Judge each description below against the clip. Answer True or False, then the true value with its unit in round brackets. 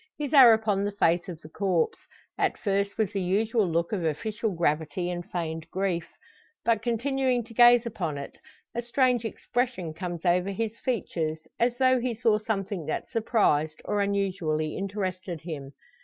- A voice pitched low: False (200 Hz)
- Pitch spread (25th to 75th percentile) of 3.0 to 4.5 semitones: False (5.2 semitones)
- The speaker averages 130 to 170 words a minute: True (165 wpm)